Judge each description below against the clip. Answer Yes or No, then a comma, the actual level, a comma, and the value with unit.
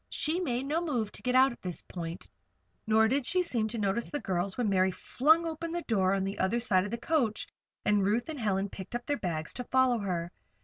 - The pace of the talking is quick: Yes, fast, 235 wpm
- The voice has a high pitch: Yes, high, 225 Hz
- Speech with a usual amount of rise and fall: No, wide, 5.8 semitones